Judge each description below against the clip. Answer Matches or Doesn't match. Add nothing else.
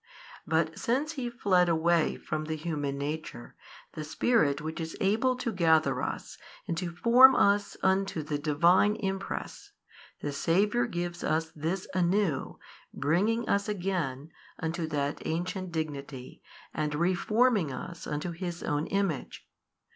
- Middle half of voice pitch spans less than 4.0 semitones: Doesn't match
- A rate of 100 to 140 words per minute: Matches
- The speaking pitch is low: Doesn't match